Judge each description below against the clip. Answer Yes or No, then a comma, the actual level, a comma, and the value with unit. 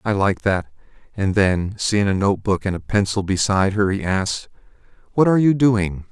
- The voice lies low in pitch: Yes, low, 100 Hz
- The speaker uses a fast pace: No, average, 185 wpm